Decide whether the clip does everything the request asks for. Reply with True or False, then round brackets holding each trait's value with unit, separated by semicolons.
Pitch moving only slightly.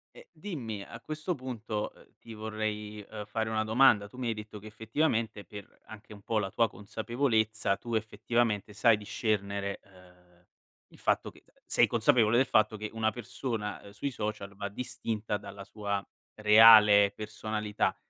True (1.8 semitones)